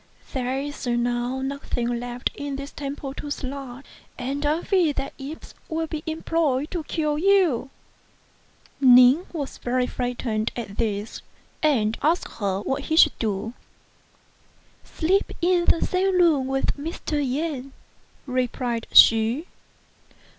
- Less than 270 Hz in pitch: No, very high, 275 Hz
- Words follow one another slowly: Yes, slow, 130 wpm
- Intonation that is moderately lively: Yes, average, 4.2 semitones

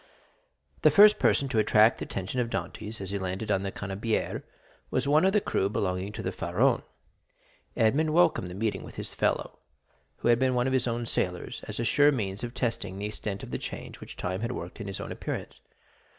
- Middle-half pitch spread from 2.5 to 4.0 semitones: No, average, 4.7 semitones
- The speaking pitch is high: No, low, 110 Hz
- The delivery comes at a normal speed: No, fast, 210 wpm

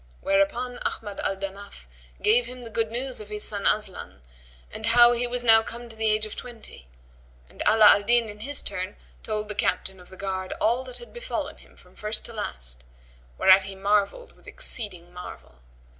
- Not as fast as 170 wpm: No, average, 195 wpm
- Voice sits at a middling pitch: No, high, 215 Hz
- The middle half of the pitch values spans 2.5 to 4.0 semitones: Yes, average, 3.5 semitones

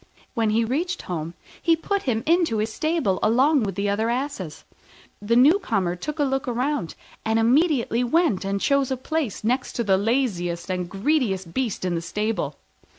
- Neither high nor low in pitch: No, high, 230 Hz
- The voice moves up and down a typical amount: No, wide, 6.2 semitones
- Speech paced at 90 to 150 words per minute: No, average, 175 wpm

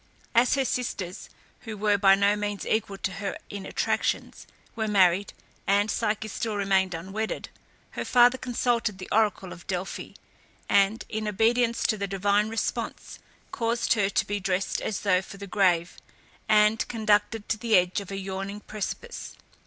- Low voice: No, high, 205 Hz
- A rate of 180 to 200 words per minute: No, average, 160 wpm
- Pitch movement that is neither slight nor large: No, narrow, 2.2 semitones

